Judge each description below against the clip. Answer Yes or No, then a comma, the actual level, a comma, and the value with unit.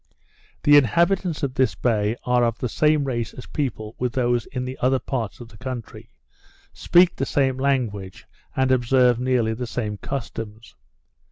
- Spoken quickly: No, average, 165 wpm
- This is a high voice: No, low, 125 Hz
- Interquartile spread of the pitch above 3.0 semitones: No, narrow, 2.6 semitones